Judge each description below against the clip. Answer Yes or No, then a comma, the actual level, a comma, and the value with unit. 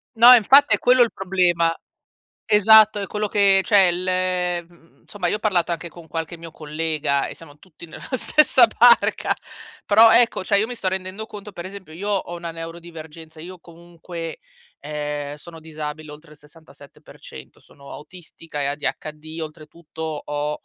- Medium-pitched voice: Yes, medium, 170 Hz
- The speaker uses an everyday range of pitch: Yes, average, 4.0 semitones